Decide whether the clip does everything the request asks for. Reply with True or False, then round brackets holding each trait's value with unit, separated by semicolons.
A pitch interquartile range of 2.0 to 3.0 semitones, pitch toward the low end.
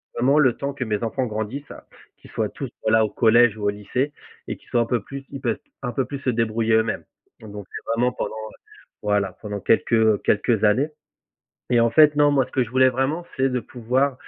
False (3.4 semitones; 120 Hz)